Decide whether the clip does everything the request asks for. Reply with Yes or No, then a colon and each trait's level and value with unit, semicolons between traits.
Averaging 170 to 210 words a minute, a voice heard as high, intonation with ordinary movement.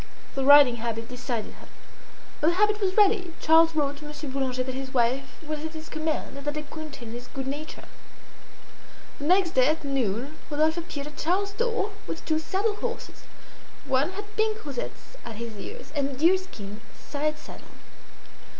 Yes: average, 180 wpm; very high, 300 Hz; average, 4.8 semitones